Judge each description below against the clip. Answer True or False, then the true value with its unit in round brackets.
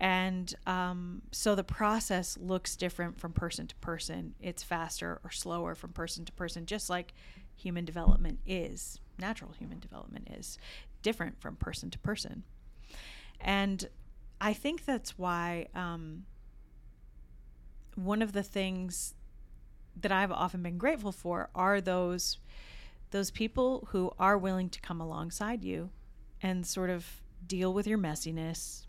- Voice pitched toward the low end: False (180 Hz)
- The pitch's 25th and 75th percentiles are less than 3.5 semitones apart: True (2.8 semitones)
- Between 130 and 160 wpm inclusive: True (140 wpm)